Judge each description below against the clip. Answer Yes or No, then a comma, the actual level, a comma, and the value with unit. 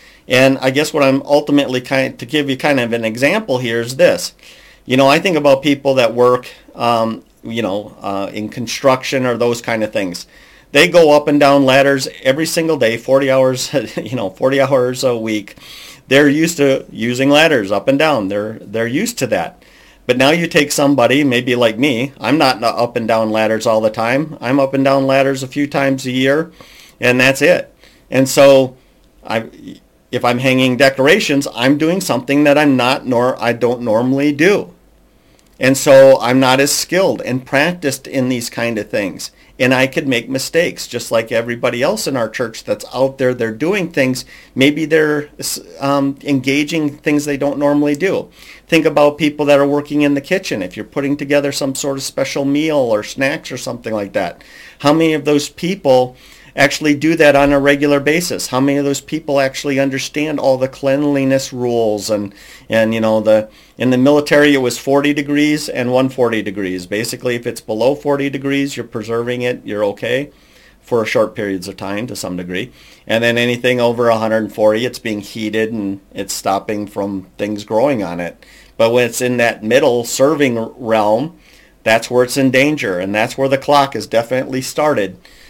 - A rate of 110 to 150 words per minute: No, average, 190 wpm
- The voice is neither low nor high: No, low, 130 Hz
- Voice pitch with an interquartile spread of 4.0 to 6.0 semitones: No, average, 3.3 semitones